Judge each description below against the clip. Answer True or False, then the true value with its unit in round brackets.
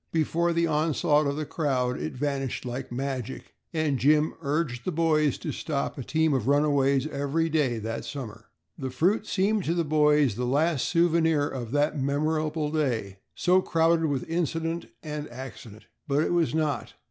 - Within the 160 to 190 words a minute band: True (170 wpm)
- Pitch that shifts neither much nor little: True (3.3 semitones)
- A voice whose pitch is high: False (150 Hz)